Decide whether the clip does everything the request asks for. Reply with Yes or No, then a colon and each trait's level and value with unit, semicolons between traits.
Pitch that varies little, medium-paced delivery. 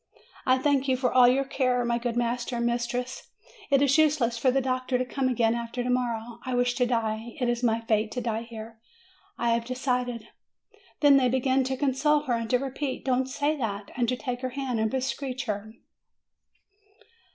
No: narrow, 1.9 semitones; fast, 210 wpm